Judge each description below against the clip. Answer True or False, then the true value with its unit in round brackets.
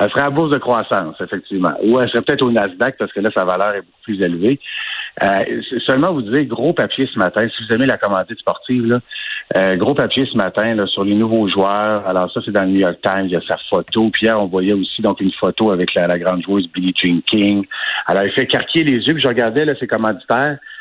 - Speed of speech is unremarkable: False (255 wpm)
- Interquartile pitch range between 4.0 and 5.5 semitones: True (4.3 semitones)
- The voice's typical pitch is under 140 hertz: True (110 Hz)